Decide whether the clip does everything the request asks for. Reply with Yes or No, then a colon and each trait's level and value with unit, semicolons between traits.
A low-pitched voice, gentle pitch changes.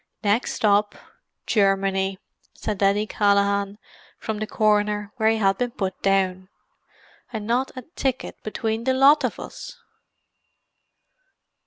No: high, 210 Hz; narrow, 2.2 semitones